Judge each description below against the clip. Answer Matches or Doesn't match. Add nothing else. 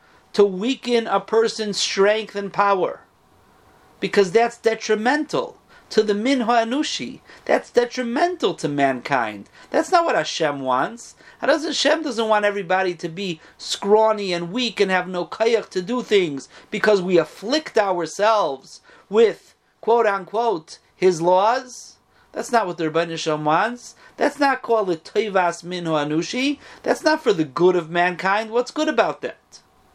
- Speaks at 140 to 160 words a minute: Matches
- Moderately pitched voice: Doesn't match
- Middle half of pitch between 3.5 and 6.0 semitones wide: Matches